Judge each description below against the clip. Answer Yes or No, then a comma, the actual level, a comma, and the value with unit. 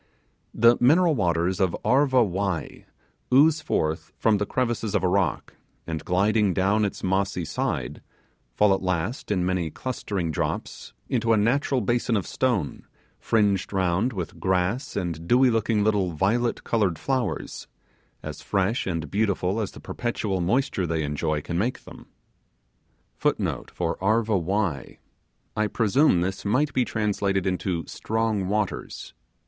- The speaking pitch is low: Yes, low, 100 Hz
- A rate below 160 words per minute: Yes, slow, 135 wpm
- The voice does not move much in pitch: No, average, 4.3 semitones